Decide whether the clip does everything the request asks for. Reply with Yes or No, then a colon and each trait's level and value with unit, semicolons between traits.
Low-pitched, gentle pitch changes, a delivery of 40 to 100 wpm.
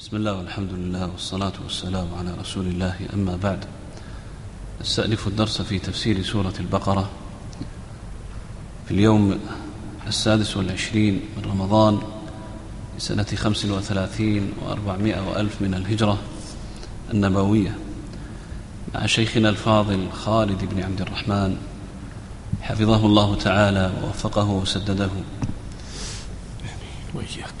Yes: low, 100 Hz; narrow, 1.8 semitones; average, 95 wpm